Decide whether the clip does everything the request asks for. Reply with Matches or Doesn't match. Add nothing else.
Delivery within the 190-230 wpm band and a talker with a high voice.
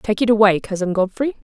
Matches